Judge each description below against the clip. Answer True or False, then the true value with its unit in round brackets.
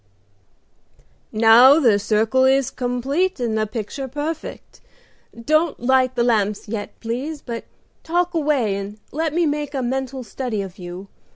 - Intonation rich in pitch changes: False (4.9 semitones)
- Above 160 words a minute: False (145 wpm)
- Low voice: False (250 Hz)